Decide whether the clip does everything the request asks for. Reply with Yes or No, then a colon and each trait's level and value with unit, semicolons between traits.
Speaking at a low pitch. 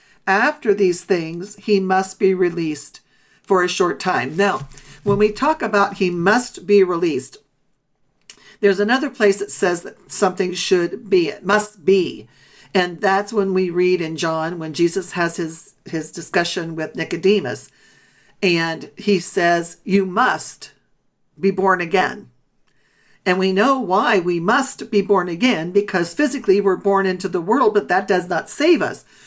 No: high, 190 Hz